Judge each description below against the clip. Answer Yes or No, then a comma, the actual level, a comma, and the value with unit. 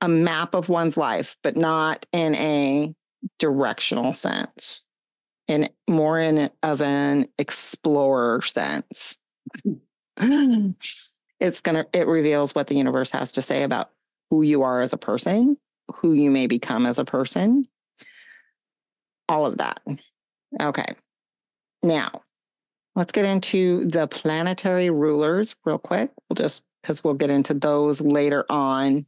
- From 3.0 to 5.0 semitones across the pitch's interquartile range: Yes, average, 3.7 semitones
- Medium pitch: Yes, medium, 155 Hz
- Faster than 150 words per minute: No, slow, 135 wpm